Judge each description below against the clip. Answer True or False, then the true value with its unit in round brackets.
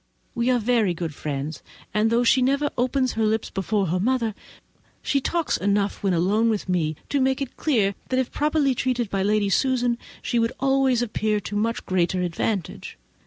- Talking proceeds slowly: False (185 wpm)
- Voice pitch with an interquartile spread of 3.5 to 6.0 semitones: True (4.7 semitones)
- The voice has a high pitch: True (225 Hz)